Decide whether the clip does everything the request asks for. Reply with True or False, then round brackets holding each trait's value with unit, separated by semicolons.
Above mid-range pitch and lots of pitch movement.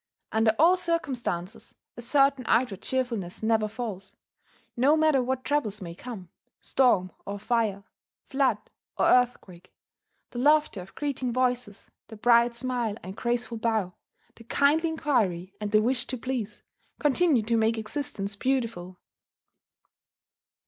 False (235 Hz; 3.9 semitones)